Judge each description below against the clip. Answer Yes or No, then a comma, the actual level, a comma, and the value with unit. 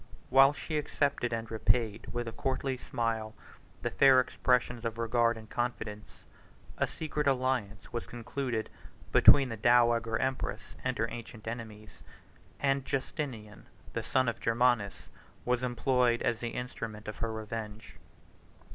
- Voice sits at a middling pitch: No, low, 120 Hz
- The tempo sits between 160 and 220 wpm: No, average, 140 wpm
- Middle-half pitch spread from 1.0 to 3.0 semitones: Yes, narrow, 2.4 semitones